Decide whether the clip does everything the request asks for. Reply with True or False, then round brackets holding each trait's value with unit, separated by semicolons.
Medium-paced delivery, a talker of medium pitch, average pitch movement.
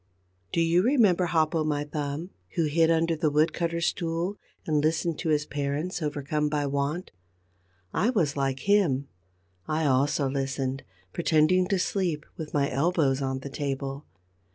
True (155 wpm; 155 Hz; 3.1 semitones)